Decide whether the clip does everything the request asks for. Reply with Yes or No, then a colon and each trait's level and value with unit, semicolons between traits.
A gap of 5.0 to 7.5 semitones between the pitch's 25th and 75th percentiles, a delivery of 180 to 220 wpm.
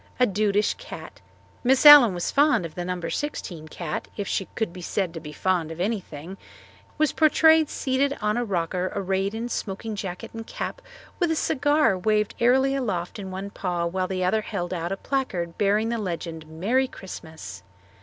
Yes: wide, 5.6 semitones; average, 185 wpm